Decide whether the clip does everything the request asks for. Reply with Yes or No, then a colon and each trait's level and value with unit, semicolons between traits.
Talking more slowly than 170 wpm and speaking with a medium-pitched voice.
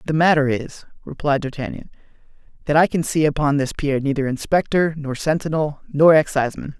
Yes: average, 160 wpm; medium, 145 Hz